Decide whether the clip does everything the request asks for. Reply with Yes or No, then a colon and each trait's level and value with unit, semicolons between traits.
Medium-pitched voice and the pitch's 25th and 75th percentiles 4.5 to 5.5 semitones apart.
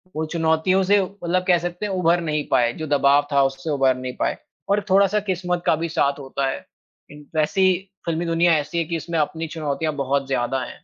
No: medium, 160 Hz; average, 3.8 semitones